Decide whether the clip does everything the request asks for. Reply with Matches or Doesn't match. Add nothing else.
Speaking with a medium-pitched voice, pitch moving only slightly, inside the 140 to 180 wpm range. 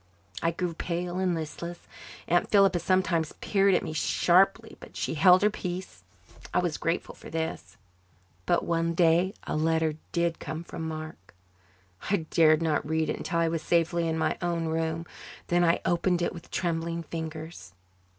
Matches